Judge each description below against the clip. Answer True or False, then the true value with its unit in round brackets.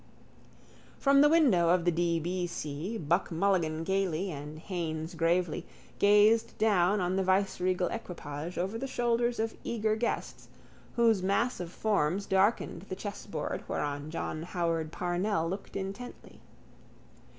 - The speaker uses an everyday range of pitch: True (3.9 semitones)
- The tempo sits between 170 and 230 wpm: False (135 wpm)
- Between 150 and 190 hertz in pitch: True (185 Hz)